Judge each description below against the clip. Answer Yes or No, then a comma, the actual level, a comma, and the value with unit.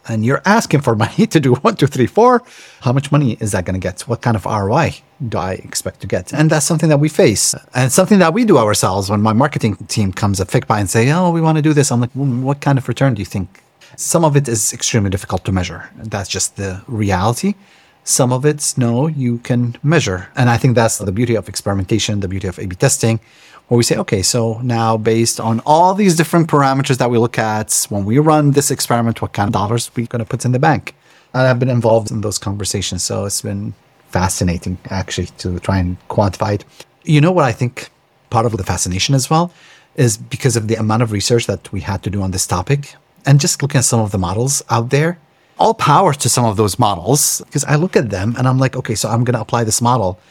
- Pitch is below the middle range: Yes, low, 120 Hz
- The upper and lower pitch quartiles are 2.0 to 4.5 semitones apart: No, average, 5.1 semitones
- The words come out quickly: Yes, fast, 250 wpm